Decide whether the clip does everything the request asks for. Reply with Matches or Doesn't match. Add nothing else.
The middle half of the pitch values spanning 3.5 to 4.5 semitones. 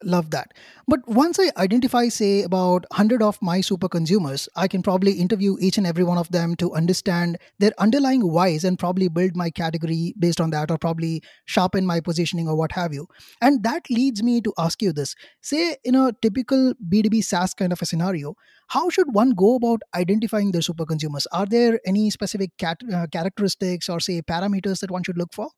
Matches